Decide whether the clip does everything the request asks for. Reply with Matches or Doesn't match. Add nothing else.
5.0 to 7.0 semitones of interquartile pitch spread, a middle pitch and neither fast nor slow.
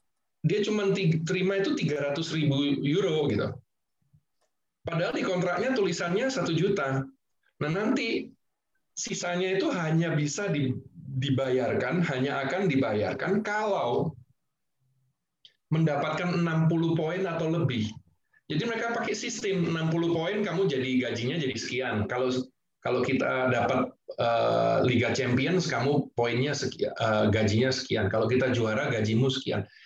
Matches